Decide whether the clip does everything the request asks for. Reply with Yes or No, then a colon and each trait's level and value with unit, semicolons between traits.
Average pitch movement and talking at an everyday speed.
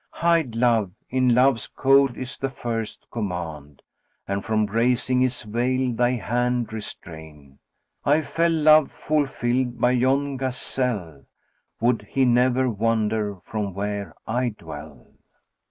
No: average, 3.6 semitones; slow, 130 wpm